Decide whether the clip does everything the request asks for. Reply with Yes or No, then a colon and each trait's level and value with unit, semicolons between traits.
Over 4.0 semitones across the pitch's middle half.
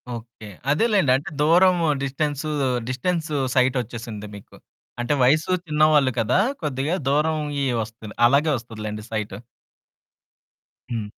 Yes: average, 5.0 semitones